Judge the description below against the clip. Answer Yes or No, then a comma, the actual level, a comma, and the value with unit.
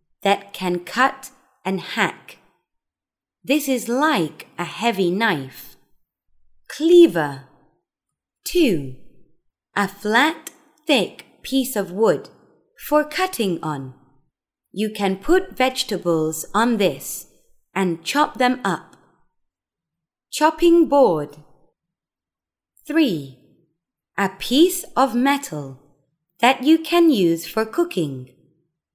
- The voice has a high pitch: Yes, high, 200 Hz